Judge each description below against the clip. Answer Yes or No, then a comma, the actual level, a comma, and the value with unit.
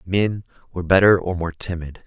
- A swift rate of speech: No, average, 175 wpm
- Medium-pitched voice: No, very low, 90 Hz